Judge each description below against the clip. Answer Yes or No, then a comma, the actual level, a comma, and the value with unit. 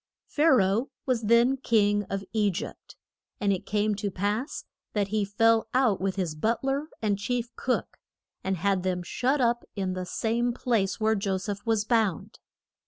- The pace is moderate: Yes, average, 180 wpm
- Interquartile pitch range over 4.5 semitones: No, average, 3.2 semitones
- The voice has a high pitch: Yes, high, 210 Hz